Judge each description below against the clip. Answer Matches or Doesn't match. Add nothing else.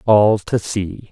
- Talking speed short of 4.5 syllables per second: Matches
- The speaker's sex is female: Doesn't match